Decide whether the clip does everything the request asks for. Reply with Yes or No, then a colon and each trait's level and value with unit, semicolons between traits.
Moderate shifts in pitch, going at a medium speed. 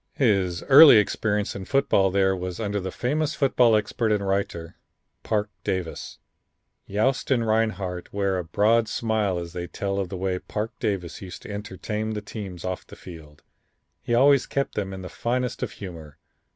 Yes: average, 3.3 semitones; average, 170 wpm